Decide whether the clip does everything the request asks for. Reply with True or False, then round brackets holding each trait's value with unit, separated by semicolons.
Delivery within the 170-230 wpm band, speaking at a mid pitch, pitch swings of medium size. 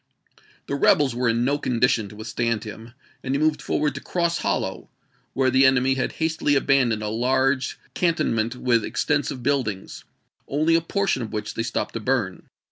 False (180 wpm; 130 Hz; 3.7 semitones)